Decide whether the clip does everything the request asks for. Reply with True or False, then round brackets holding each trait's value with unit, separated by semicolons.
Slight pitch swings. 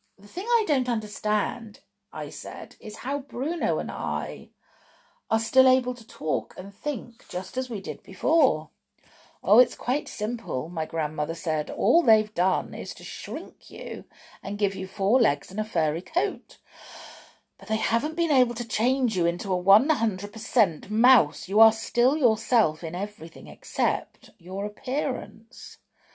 False (4.7 semitones)